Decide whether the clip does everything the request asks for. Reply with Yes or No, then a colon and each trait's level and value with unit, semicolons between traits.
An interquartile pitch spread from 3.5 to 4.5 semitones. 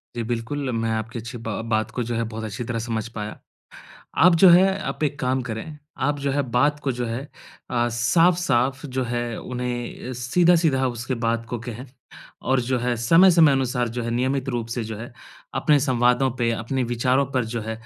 No: narrow, 2.5 semitones